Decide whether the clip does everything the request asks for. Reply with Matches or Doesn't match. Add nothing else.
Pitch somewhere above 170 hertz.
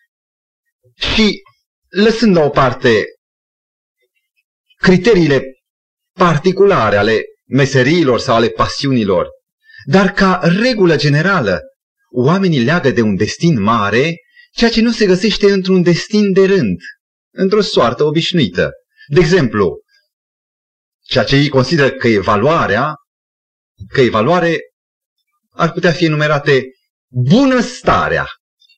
Matches